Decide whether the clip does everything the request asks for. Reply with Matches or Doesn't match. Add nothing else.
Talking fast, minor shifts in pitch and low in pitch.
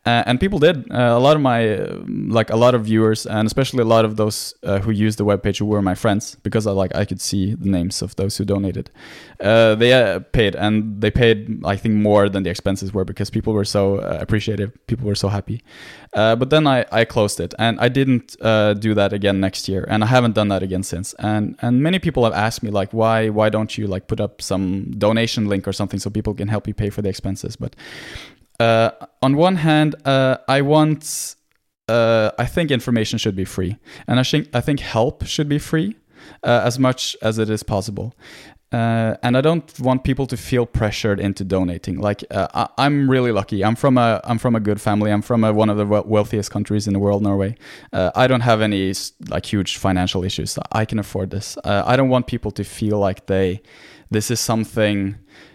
Doesn't match